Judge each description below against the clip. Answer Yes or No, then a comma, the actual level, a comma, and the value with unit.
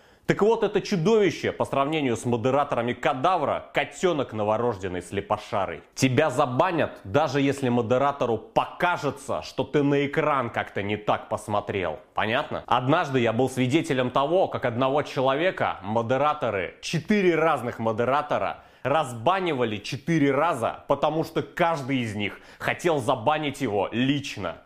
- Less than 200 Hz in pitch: Yes, medium, 140 Hz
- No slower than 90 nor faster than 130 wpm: Yes, average, 125 wpm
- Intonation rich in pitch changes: No, average, 4.6 semitones